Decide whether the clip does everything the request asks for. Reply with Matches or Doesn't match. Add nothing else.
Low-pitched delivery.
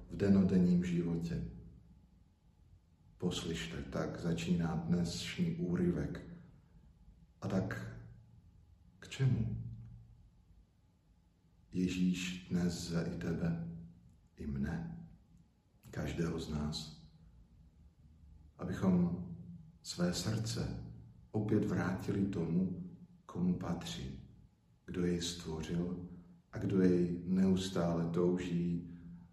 Matches